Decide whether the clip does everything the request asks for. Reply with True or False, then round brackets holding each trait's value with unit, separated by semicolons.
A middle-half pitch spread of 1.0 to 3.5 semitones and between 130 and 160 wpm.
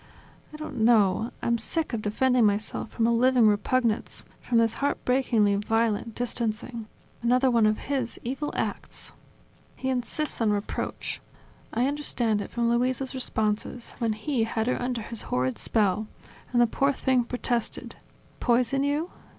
True (2.7 semitones; 150 wpm)